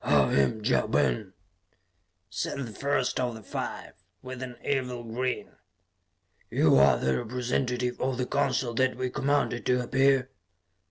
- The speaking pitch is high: No, low, 125 Hz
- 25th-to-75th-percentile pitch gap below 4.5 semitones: Yes, narrow, 2.6 semitones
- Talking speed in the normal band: Yes, average, 145 wpm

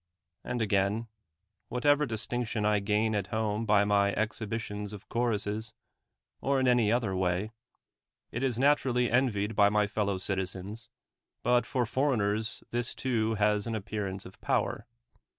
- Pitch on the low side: Yes, low, 110 Hz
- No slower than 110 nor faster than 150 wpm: Yes, average, 145 wpm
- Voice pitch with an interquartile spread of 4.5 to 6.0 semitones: No, average, 2.7 semitones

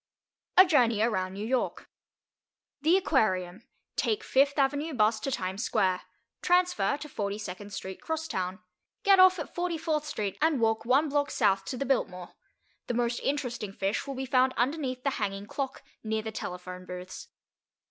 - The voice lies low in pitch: No, high, 245 Hz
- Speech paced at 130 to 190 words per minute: Yes, average, 155 wpm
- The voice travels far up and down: Yes, wide, 6.7 semitones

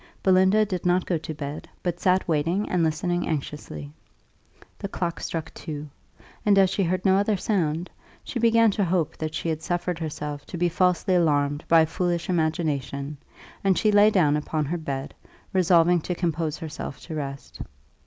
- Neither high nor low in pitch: Yes, medium, 170 Hz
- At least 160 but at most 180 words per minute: Yes, average, 175 wpm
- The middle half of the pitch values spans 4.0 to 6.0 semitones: No, average, 3.3 semitones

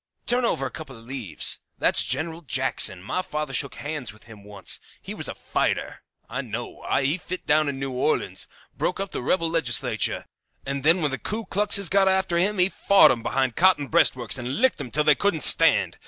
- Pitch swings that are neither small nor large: No, wide, 6.1 semitones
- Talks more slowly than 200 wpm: No, fast, 205 wpm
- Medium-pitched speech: Yes, medium, 150 Hz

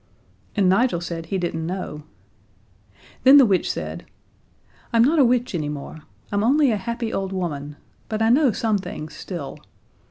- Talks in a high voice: Yes, high, 195 Hz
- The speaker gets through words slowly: No, average, 160 wpm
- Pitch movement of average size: No, wide, 5.8 semitones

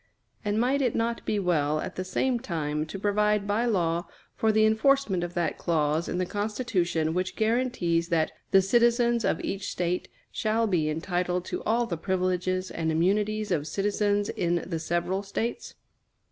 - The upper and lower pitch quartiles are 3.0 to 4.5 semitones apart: Yes, average, 4.1 semitones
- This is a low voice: No, high, 190 Hz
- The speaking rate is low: No, average, 170 wpm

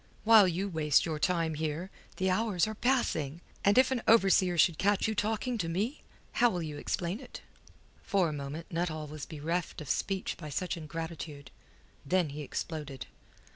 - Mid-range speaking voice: Yes, medium, 170 Hz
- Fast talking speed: No, average, 170 wpm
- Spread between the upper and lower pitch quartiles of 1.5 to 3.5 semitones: No, average, 4.6 semitones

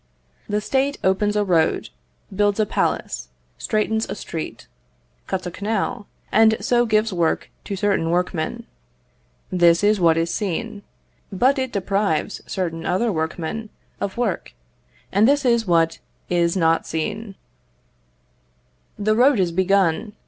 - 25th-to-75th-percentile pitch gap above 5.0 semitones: No, average, 4.2 semitones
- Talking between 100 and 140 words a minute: Yes, slow, 135 wpm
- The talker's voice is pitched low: No, high, 200 Hz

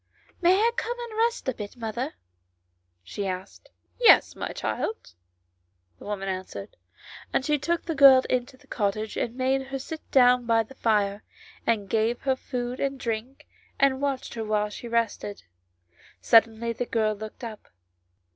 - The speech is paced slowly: No, average, 175 wpm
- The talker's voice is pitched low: No, high, 240 Hz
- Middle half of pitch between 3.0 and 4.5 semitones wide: Yes, average, 4.1 semitones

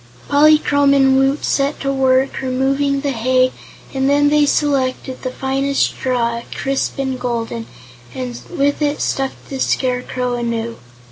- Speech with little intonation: Yes, narrow, 1.6 semitones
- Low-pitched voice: No, very high, 265 Hz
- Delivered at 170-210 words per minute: No, average, 140 wpm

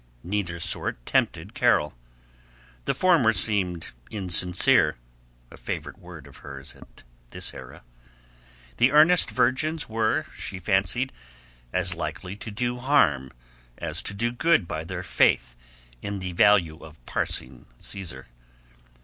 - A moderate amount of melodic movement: No, wide, 6.7 semitones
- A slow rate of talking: Yes, slow, 125 wpm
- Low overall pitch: Yes, very low, 95 Hz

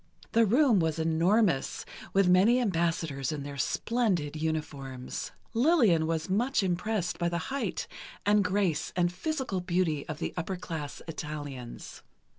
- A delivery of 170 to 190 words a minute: No, slow, 135 wpm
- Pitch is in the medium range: Yes, medium, 175 Hz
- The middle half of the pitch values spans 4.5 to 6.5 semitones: Yes, average, 4.9 semitones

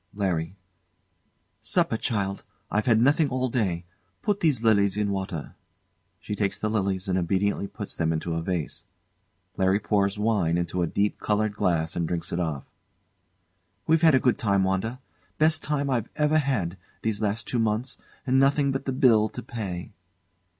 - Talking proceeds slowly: No, average, 170 wpm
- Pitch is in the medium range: No, low, 105 Hz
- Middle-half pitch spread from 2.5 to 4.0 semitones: No, average, 5.1 semitones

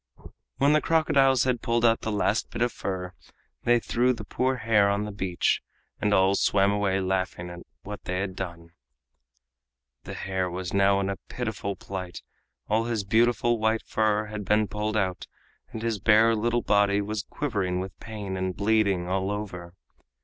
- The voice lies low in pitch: Yes, low, 105 Hz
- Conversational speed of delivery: Yes, average, 175 wpm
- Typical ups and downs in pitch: Yes, average, 3.0 semitones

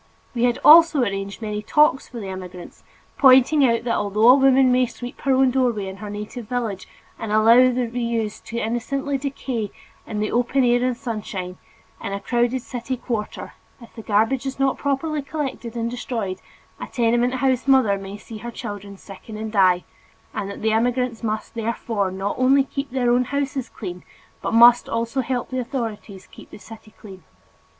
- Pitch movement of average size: Yes, average, 3.4 semitones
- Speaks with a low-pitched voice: No, high, 235 Hz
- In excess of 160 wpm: Yes, average, 185 wpm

